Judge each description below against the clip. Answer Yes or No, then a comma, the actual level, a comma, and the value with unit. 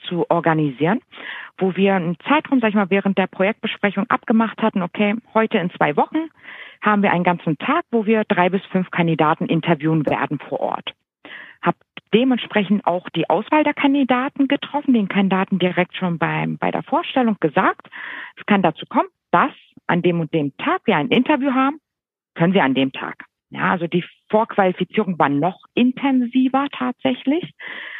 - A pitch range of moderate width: No, wide, 6.7 semitones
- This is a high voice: Yes, high, 205 Hz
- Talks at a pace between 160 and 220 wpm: Yes, average, 165 wpm